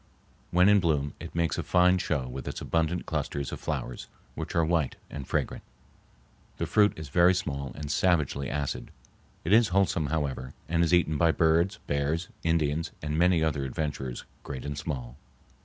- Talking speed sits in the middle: Yes, average, 175 wpm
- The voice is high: No, very low, 80 Hz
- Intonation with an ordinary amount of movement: Yes, average, 3.4 semitones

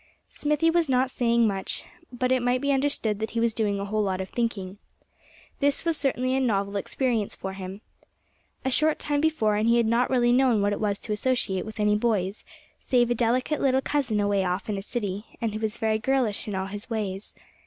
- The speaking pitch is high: Yes, high, 225 Hz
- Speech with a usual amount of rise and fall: Yes, average, 3.9 semitones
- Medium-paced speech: No, fast, 215 wpm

